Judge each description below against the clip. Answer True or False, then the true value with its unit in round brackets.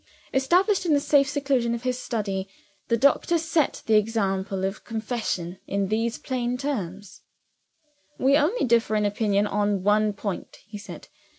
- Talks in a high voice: True (225 Hz)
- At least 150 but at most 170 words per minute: True (155 wpm)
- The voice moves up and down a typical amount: True (4.8 semitones)